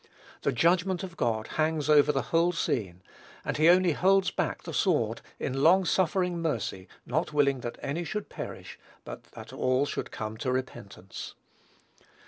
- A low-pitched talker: No, medium, 150 Hz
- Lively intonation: Yes, wide, 6.0 semitones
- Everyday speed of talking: Yes, average, 160 wpm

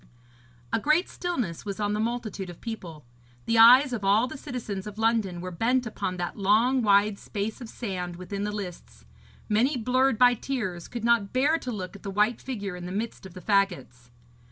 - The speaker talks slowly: No, average, 200 wpm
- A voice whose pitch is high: Yes, high, 210 Hz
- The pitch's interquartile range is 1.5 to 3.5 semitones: No, average, 4.1 semitones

